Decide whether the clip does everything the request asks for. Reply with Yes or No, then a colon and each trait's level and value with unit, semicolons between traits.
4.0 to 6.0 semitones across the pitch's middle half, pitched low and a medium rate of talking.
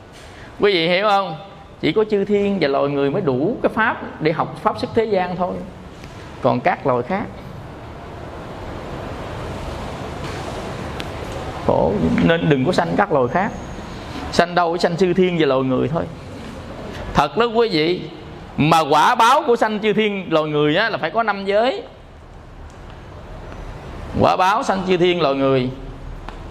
No: average, 5.0 semitones; medium, 180 Hz; average, 160 wpm